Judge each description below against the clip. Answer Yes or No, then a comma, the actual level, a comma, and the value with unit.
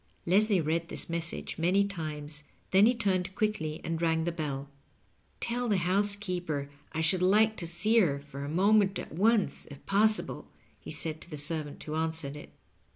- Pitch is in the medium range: Yes, medium, 170 Hz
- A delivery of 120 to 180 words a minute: Yes, average, 175 wpm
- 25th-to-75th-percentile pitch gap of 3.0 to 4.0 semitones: No, average, 4.4 semitones